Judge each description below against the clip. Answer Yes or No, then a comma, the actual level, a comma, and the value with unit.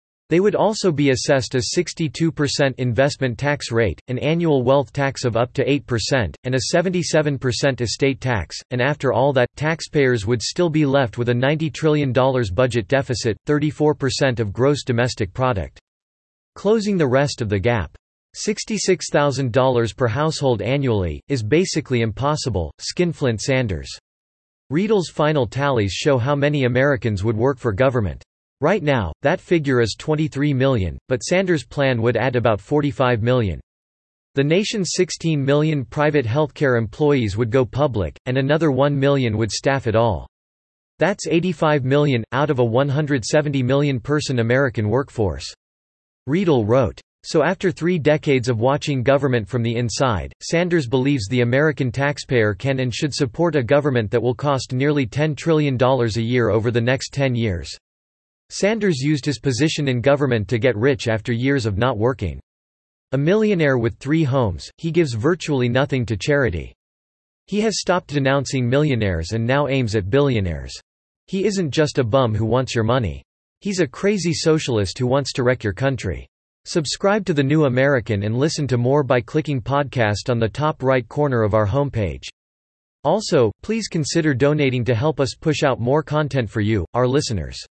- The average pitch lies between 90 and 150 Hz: Yes, low, 135 Hz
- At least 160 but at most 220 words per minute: Yes, average, 165 wpm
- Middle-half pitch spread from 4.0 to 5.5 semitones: Yes, average, 4.4 semitones